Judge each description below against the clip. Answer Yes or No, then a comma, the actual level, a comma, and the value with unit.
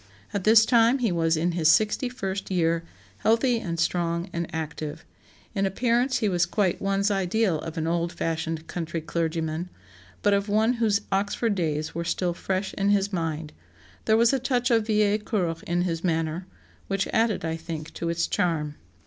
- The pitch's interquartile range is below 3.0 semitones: No, average, 4.4 semitones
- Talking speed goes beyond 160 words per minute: Yes, average, 180 wpm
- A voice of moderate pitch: Yes, medium, 180 Hz